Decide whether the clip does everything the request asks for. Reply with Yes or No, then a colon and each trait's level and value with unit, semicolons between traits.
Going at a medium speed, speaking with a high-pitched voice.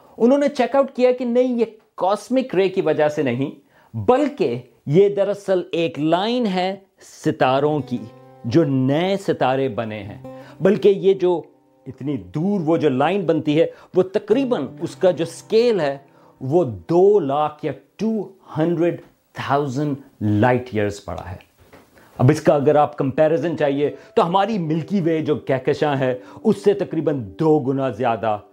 No: average, 155 wpm; medium, 155 Hz